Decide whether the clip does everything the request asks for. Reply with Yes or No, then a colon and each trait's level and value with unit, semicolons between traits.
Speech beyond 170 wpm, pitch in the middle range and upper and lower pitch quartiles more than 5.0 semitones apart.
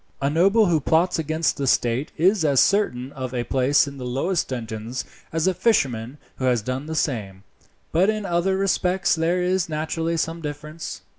Yes: average, 180 wpm; medium, 155 Hz; wide, 5.4 semitones